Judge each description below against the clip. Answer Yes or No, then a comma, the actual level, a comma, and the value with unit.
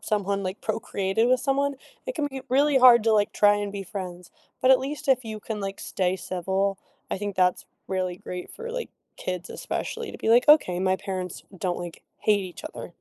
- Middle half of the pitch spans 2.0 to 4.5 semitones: No, wide, 5.5 semitones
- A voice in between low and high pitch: No, high, 205 Hz